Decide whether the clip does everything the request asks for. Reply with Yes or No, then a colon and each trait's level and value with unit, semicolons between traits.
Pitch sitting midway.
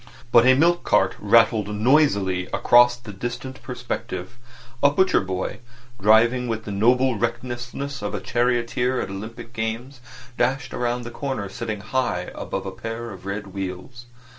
No: low, 120 Hz